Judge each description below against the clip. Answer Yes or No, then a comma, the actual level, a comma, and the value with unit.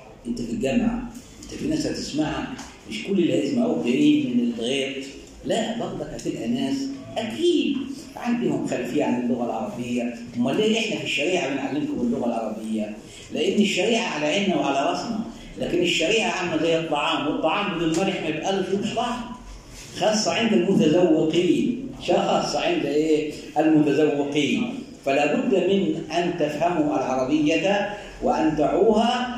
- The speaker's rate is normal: No, slow, 130 wpm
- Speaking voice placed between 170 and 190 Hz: Yes, medium, 185 Hz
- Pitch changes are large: Yes, wide, 8.0 semitones